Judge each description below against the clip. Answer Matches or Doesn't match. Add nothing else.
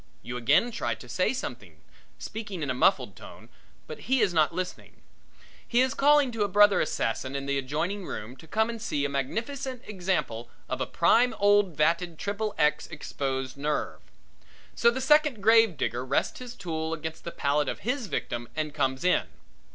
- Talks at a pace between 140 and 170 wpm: Doesn't match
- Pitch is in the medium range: Matches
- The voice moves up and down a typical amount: Doesn't match